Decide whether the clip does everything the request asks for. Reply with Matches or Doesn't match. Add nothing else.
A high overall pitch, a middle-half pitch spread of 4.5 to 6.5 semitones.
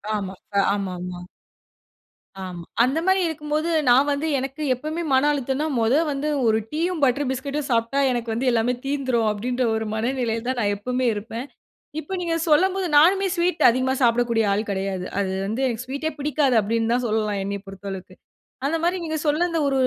Matches